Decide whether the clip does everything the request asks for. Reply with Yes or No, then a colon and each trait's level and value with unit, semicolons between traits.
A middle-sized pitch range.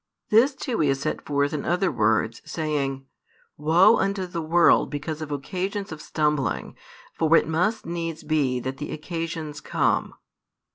Yes: average, 3.2 semitones